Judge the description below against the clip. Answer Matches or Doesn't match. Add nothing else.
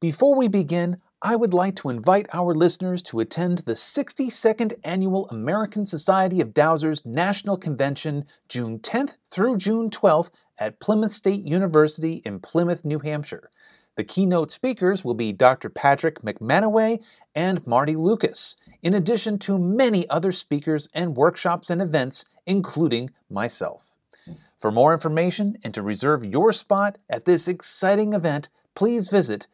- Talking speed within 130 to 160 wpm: Matches